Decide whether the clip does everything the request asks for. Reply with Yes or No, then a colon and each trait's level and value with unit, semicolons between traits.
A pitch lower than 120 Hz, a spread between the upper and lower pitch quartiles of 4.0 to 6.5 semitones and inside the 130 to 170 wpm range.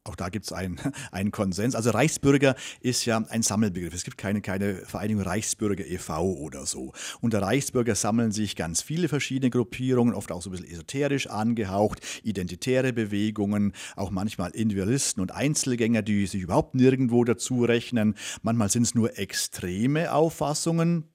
Yes: low, 110 Hz; average, 4.4 semitones; average, 160 wpm